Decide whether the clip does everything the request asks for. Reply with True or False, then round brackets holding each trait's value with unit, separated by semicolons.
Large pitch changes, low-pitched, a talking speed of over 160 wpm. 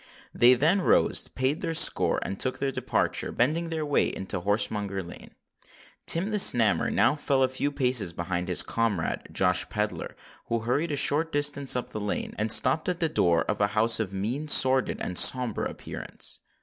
True (6.1 semitones; 125 Hz; 180 wpm)